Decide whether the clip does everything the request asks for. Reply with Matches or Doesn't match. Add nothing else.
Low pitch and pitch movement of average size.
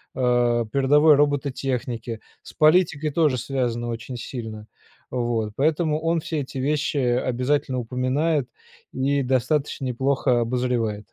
Matches